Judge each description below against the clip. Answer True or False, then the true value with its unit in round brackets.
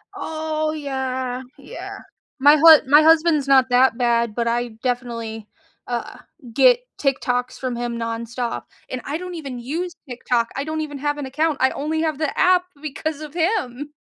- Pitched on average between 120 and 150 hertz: False (275 Hz)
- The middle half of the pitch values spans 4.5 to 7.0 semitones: False (4.1 semitones)